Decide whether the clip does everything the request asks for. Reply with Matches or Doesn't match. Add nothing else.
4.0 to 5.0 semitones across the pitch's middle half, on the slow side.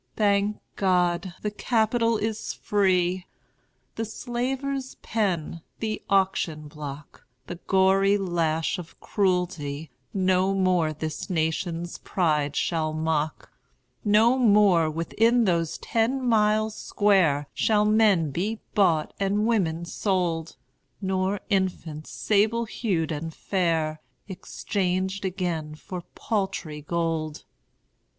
Matches